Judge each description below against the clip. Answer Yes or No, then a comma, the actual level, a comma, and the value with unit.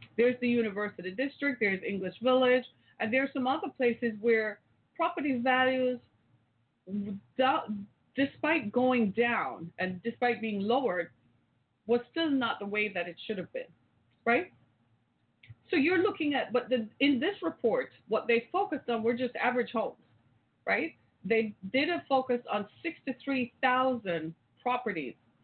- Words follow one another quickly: No, average, 140 wpm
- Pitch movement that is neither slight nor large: Yes, average, 4.7 semitones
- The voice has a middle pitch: No, high, 235 Hz